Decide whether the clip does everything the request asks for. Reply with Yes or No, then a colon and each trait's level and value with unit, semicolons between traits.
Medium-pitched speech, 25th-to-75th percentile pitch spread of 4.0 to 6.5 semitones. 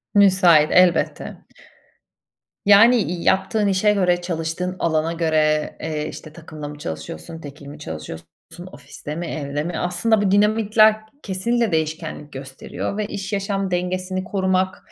Yes: medium, 175 Hz; average, 4.3 semitones